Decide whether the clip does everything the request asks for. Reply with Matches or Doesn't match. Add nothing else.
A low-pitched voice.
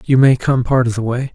Matches